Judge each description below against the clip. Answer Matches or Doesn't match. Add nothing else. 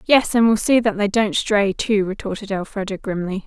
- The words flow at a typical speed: Doesn't match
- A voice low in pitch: Doesn't match